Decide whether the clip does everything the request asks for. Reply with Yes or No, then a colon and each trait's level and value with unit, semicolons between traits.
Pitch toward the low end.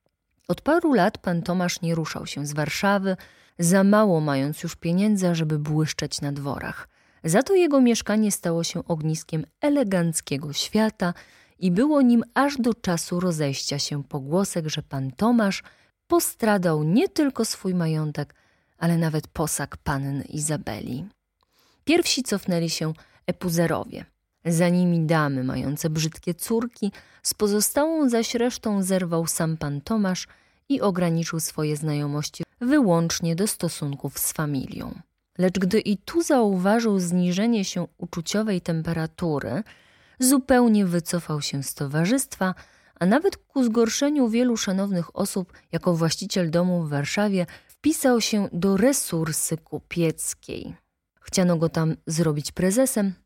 No: medium, 175 Hz